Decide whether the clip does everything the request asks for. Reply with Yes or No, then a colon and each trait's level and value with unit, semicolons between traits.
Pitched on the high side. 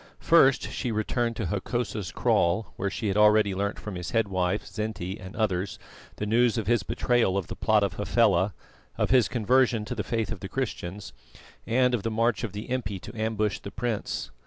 No: low, 105 Hz